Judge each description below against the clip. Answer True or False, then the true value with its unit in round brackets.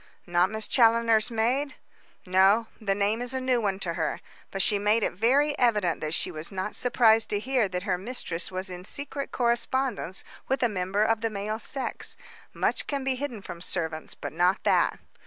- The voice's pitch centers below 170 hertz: False (215 Hz)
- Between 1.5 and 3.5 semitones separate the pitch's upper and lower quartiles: False (4.6 semitones)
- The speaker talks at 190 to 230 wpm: True (195 wpm)